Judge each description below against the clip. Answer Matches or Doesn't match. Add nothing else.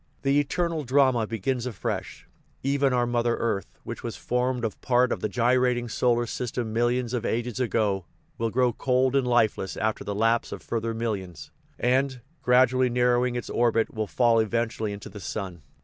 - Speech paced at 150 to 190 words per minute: Matches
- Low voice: Matches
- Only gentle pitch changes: Matches